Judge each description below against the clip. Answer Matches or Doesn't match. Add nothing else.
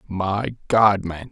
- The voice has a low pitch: Matches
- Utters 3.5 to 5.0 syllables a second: Doesn't match